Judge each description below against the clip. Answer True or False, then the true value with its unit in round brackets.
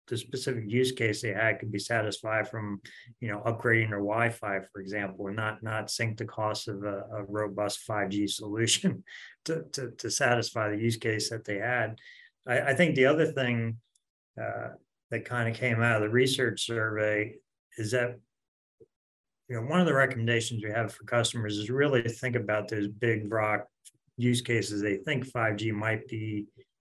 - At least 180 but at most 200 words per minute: True (190 wpm)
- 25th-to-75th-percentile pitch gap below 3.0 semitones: True (2.4 semitones)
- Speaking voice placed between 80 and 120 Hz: True (115 Hz)